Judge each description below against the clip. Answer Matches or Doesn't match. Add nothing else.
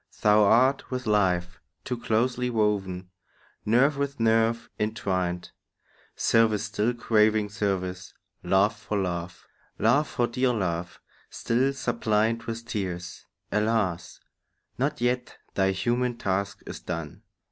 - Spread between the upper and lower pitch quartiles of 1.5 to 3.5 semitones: Doesn't match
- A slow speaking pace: Matches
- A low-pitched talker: Matches